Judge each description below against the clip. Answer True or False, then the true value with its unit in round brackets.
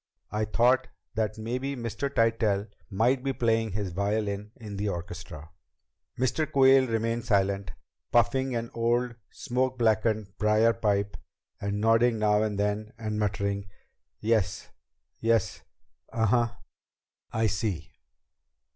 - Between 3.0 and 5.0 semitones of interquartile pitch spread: False (2.5 semitones)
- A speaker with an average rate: False (125 wpm)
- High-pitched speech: False (110 Hz)